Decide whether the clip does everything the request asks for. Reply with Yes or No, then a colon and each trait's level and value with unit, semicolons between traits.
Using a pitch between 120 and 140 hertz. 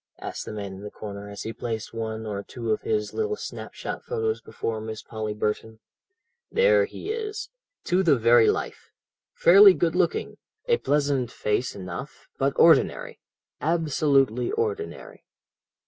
Yes: low, 135 Hz